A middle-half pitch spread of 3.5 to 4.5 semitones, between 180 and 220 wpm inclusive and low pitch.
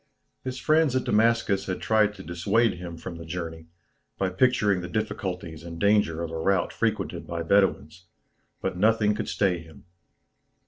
No: average, 4.2 semitones; average, 165 wpm; very low, 95 Hz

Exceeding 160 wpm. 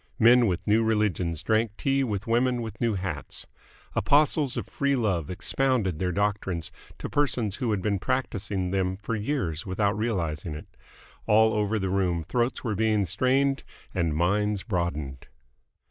No: average, 155 wpm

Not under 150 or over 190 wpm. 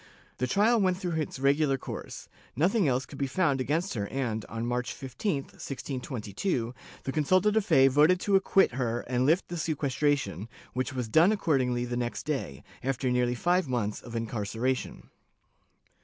Yes: average, 165 wpm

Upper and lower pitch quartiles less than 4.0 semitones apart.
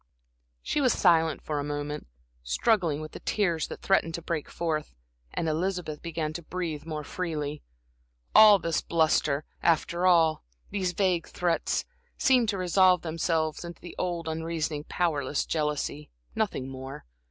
Yes: average, 2.8 semitones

